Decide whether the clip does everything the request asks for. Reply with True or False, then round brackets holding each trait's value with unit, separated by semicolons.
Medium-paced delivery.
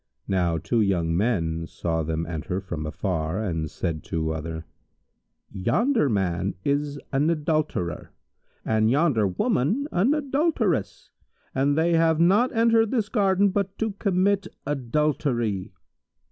False (130 wpm)